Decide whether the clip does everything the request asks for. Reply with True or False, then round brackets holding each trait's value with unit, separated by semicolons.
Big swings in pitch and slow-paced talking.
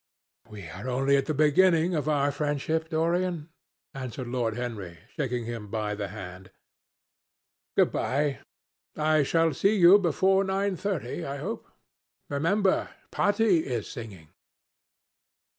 True (6.4 semitones; 125 wpm)